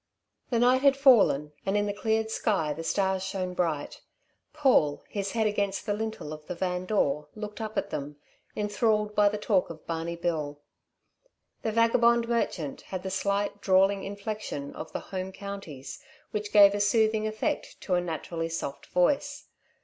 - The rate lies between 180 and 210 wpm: No, average, 170 wpm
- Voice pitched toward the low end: No, high, 200 Hz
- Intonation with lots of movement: No, average, 4.1 semitones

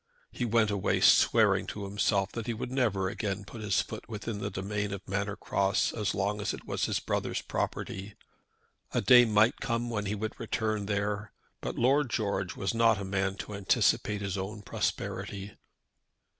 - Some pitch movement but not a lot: No, narrow, 2.2 semitones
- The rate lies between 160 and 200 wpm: Yes, average, 180 wpm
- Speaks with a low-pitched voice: Yes, low, 105 Hz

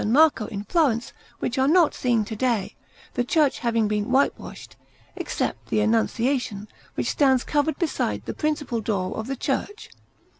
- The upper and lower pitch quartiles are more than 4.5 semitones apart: Yes, average, 4.9 semitones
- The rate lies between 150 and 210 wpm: Yes, average, 155 wpm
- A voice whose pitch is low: No, high, 245 Hz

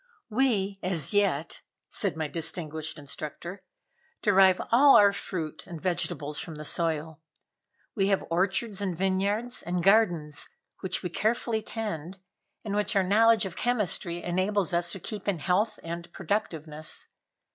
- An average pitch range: Yes, average, 3.8 semitones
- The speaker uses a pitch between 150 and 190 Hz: Yes, medium, 185 Hz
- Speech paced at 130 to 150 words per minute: Yes, average, 140 wpm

